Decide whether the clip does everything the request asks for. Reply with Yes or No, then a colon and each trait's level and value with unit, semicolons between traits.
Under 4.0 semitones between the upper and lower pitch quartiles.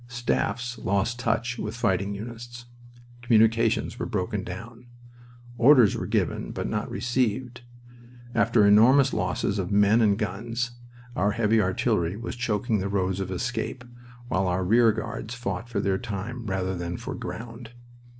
Yes: average, 3.2 semitones